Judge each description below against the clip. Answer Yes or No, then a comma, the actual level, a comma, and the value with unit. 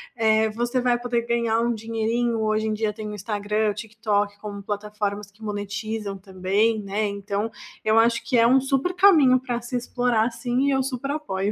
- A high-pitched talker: Yes, high, 220 Hz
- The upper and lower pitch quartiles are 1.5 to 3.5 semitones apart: Yes, narrow, 2.6 semitones